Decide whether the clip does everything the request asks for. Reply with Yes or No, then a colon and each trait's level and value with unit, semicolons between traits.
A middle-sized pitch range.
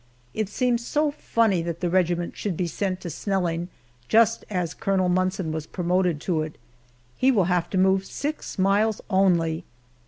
Yes: average, 3.1 semitones